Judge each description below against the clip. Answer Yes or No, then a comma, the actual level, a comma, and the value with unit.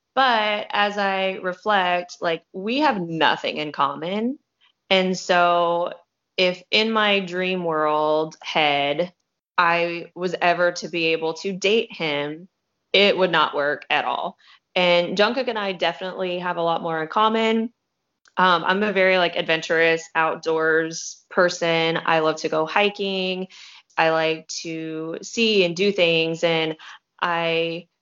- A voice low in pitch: No, medium, 175 Hz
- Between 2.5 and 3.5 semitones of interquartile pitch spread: Yes, average, 2.8 semitones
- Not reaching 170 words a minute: Yes, average, 140 wpm